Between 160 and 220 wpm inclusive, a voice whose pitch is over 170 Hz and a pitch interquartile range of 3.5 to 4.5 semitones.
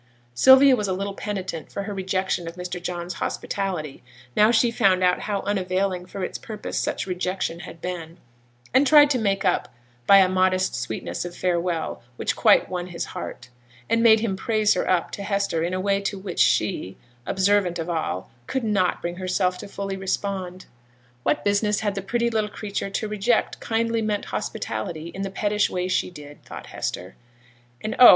No: average, 185 wpm; high, 190 Hz; narrow, 2.6 semitones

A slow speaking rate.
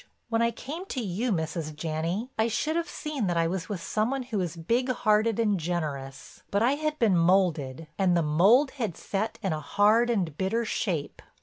No: fast, 205 wpm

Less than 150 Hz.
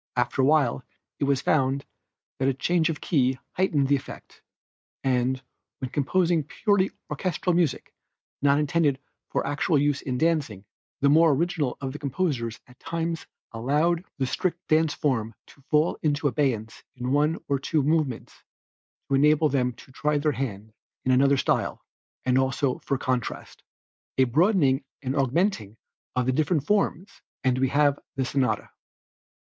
Yes: medium, 140 Hz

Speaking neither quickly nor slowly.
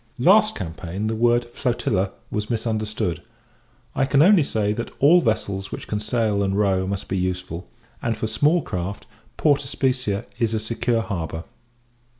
Yes: average, 155 wpm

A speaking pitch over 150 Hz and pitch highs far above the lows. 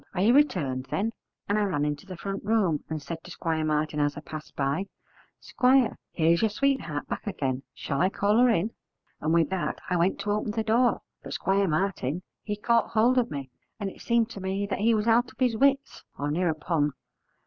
Yes: high, 190 Hz; wide, 6.3 semitones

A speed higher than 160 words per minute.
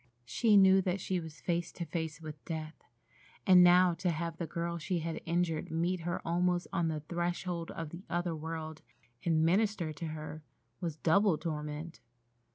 Yes: average, 170 wpm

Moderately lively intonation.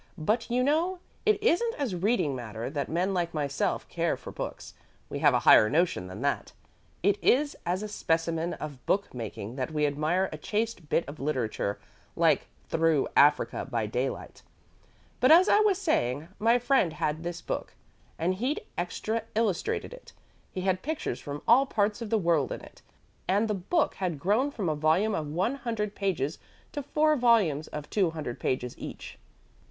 No: wide, 7.5 semitones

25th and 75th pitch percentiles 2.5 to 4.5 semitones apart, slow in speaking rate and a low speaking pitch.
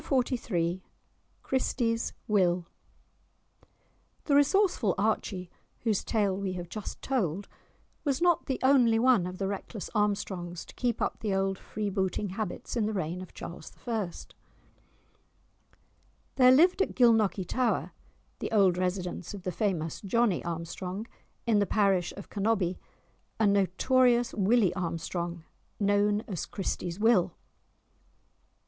No: average, 4.2 semitones; slow, 130 wpm; high, 200 Hz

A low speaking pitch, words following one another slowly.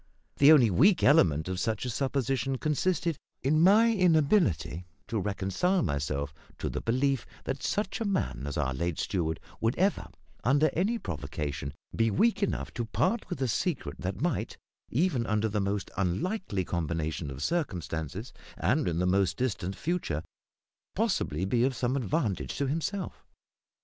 No: low, 115 Hz; average, 155 wpm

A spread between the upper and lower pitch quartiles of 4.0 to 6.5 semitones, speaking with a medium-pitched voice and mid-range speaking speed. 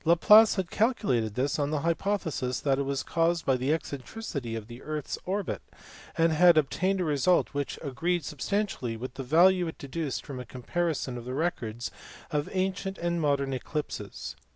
Yes: average, 5.0 semitones; medium, 150 Hz; average, 175 wpm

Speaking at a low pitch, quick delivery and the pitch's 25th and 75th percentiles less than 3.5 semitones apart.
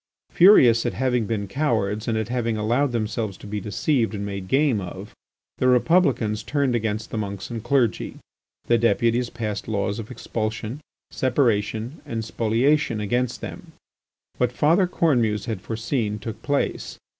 No: low, 115 Hz; average, 150 wpm; average, 3.1 semitones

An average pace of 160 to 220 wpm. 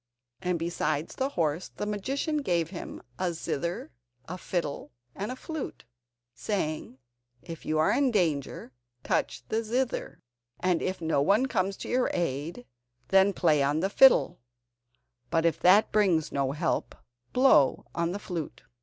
No: average, 150 wpm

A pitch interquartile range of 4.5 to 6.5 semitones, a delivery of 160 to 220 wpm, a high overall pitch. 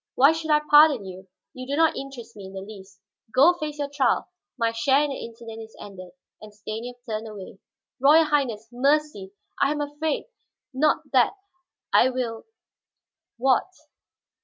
Yes: average, 5.2 semitones; average, 165 wpm; very high, 255 Hz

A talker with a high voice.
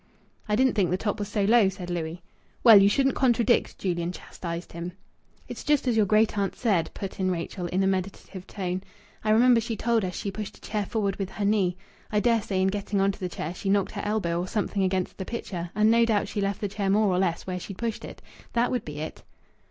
Yes: high, 200 Hz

